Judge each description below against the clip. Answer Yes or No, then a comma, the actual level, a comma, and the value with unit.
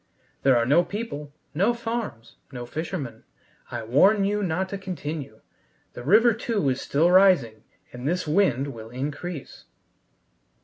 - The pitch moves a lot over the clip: Yes, wide, 7.2 semitones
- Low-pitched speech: No, medium, 160 Hz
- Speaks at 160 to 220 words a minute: No, average, 140 wpm